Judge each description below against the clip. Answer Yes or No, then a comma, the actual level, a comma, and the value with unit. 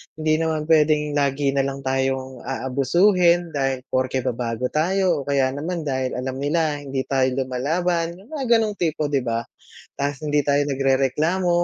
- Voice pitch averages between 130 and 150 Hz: Yes, medium, 140 Hz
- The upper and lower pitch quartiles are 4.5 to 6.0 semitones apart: No, average, 3.7 semitones